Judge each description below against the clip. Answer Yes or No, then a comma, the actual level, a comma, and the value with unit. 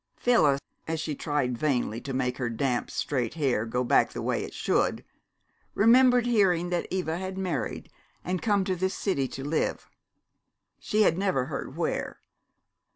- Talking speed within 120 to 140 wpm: No, average, 160 wpm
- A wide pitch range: Yes, wide, 6.3 semitones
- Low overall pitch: No, medium, 160 Hz